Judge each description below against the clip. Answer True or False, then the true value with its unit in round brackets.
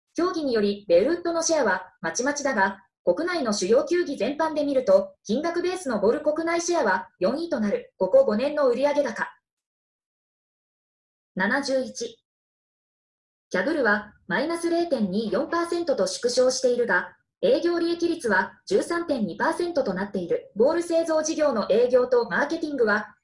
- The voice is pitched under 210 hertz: False (285 Hz)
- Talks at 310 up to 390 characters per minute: False (280 characters per minute)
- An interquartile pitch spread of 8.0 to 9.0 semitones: True (8.3 semitones)